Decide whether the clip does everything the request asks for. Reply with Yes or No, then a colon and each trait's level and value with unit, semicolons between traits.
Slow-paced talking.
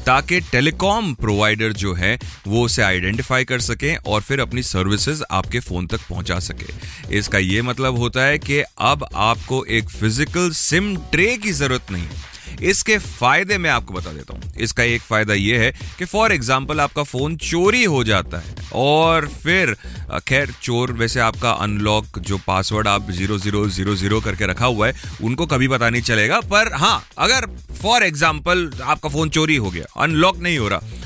No: average, 180 wpm